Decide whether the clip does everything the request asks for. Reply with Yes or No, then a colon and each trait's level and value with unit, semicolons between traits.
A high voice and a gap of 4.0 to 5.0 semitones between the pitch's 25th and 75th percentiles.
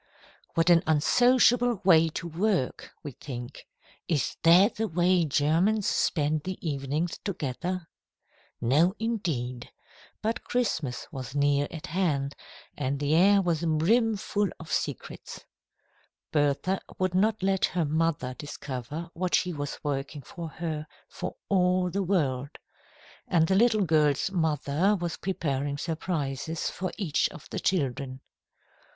No: medium, 165 Hz; average, 4.6 semitones